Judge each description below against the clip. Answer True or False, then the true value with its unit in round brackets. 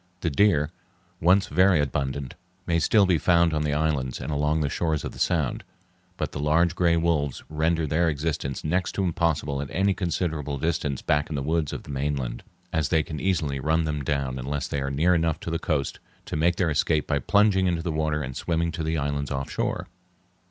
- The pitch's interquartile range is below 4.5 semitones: True (2.8 semitones)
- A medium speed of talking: False (210 wpm)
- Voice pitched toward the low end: True (80 Hz)